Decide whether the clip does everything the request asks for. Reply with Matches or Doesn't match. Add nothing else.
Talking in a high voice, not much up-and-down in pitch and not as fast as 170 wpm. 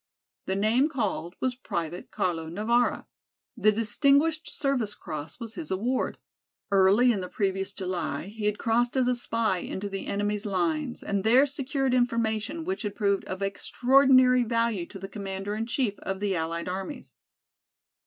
Doesn't match